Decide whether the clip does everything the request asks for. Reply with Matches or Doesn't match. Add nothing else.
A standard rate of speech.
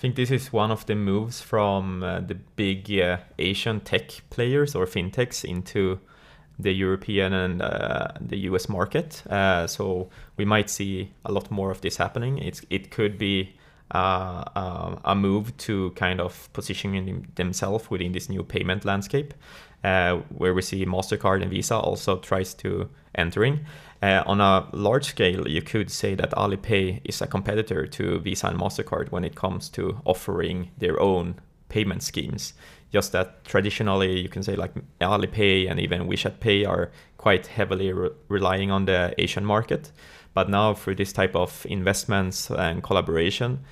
Matches